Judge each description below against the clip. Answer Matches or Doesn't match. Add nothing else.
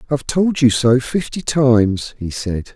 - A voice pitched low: Matches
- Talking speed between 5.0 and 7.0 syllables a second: Doesn't match